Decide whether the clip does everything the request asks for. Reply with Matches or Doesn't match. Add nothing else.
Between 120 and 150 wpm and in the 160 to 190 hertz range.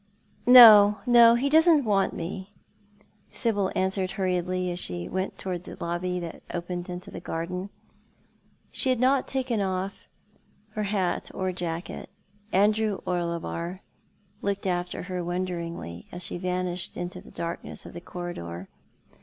Matches